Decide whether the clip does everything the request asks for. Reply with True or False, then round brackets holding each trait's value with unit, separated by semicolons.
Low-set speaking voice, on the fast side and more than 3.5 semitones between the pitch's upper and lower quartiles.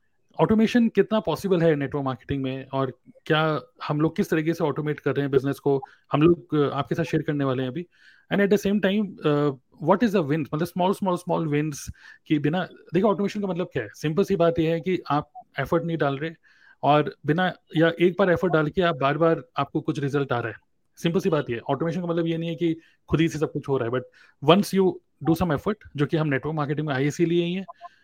False (160 Hz; 240 wpm; 3.9 semitones)